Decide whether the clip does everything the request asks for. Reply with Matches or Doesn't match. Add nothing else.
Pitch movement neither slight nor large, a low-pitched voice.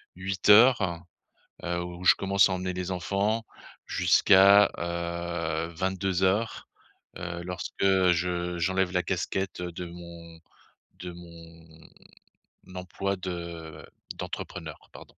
Doesn't match